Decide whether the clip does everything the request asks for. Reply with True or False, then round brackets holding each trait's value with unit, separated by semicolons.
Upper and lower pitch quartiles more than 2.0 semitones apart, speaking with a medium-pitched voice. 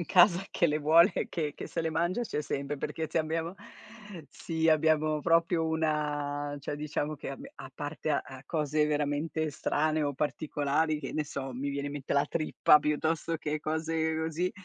False (1.7 semitones; 155 Hz)